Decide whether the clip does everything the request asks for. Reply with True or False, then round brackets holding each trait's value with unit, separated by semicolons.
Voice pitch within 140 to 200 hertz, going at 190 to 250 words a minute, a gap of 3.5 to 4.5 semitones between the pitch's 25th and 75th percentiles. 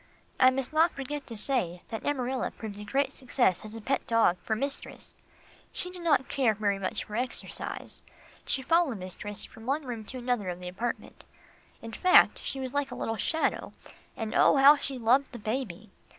False (245 Hz; 195 wpm; 4.2 semitones)